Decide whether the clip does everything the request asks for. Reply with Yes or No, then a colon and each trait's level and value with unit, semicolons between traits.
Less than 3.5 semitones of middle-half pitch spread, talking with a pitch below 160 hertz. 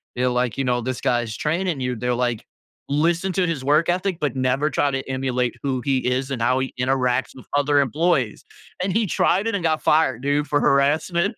No: average, 4.0 semitones; low, 135 Hz